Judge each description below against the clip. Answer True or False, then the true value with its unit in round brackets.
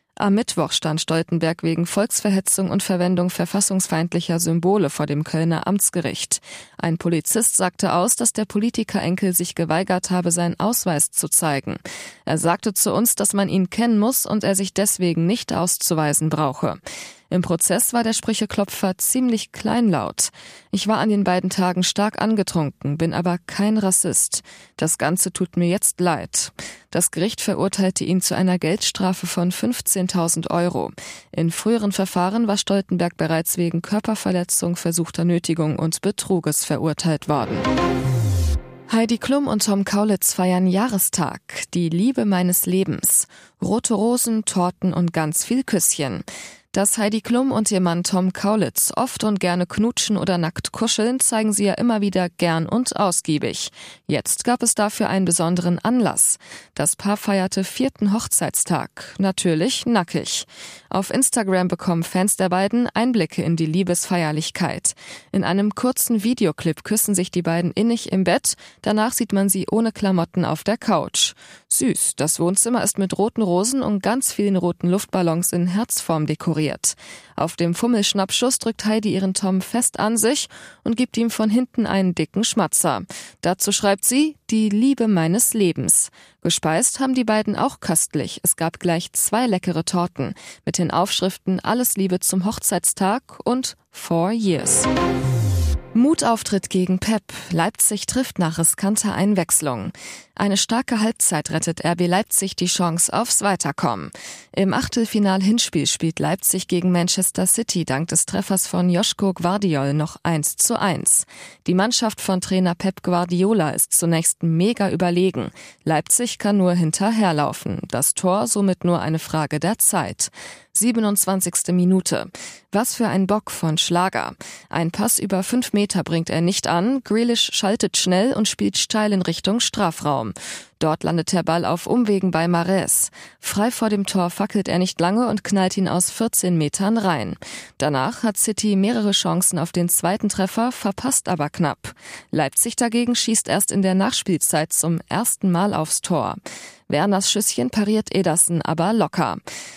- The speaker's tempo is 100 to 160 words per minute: True (150 wpm)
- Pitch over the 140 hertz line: True (190 Hz)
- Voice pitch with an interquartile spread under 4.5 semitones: True (3.8 semitones)